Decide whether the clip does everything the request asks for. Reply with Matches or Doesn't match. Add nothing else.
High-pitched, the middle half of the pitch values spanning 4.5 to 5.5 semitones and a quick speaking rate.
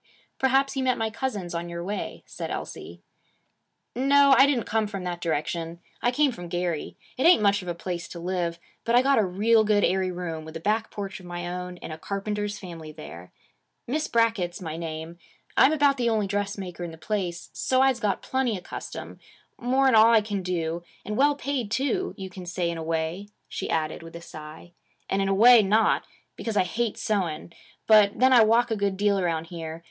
Matches